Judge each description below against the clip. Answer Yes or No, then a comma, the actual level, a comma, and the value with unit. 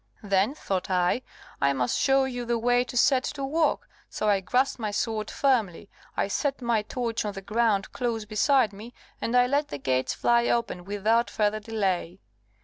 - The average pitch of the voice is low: No, high, 225 Hz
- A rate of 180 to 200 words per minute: Yes, average, 185 wpm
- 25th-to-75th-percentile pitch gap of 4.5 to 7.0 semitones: No, average, 3.8 semitones